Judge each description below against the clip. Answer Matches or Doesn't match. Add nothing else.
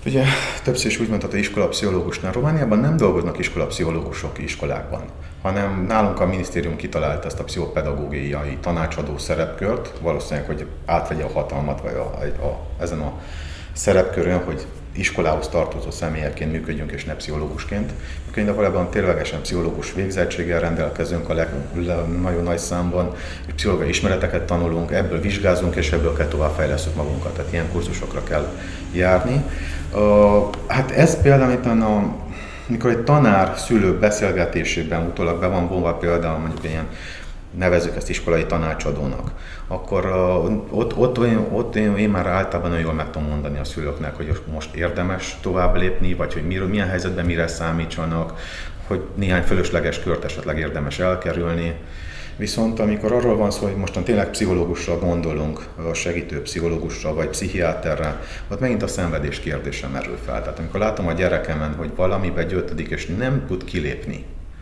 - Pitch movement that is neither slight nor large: Matches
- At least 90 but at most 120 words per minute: Doesn't match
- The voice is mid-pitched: Doesn't match